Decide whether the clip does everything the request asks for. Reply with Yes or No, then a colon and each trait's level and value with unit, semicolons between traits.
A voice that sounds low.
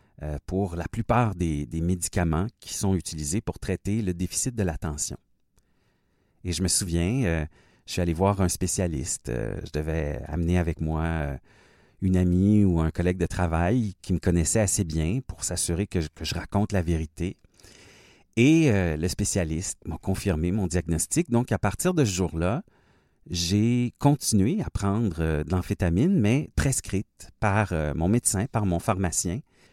Yes: very low, 90 Hz